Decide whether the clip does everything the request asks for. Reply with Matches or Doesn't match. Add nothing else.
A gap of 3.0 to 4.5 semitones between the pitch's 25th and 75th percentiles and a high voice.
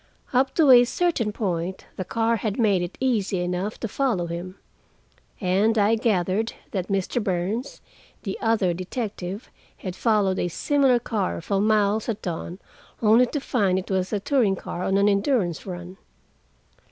Matches